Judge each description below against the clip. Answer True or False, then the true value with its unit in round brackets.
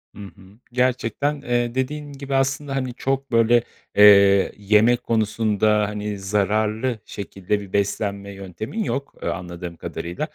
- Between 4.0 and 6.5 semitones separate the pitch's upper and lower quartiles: True (4.4 semitones)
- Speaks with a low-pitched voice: True (110 Hz)